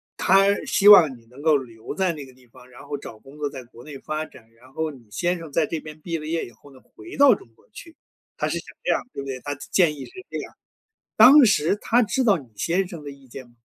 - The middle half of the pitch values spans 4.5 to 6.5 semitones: Yes, average, 5.3 semitones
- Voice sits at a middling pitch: Yes, medium, 150 Hz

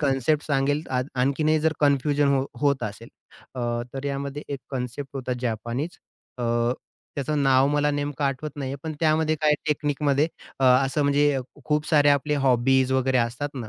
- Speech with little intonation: Yes, narrow, 2.1 semitones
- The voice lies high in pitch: No, medium, 140 Hz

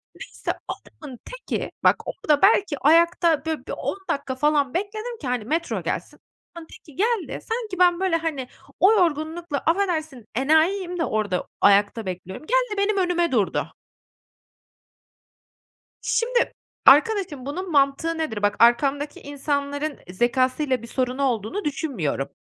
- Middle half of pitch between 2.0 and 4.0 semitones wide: No, wide, 5.5 semitones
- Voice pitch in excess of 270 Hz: Yes, very high, 305 Hz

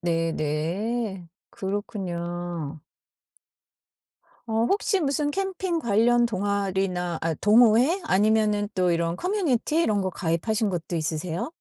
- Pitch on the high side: Yes, high, 200 Hz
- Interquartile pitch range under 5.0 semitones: No, wide, 5.5 semitones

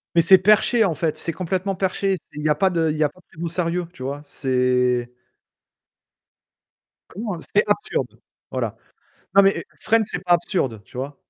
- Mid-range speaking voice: Yes, medium, 170 Hz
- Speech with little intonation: No, average, 4.8 semitones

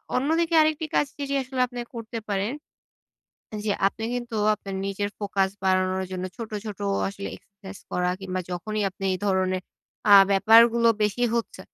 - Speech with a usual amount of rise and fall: Yes, average, 3.7 semitones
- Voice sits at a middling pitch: No, high, 205 Hz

